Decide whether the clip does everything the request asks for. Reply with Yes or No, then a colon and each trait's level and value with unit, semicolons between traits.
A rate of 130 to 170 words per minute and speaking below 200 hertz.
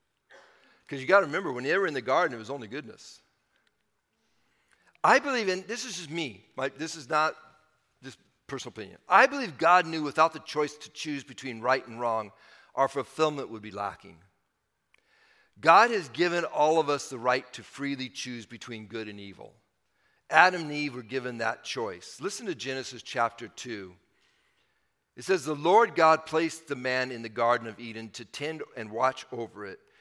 No: average, 185 wpm; low, 135 Hz